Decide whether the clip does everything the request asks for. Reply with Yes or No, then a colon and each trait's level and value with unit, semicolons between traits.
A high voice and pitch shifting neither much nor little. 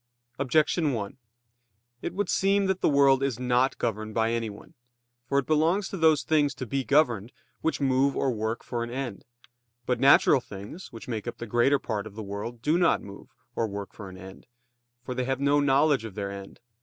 No: low, 125 Hz; average, 4.5 semitones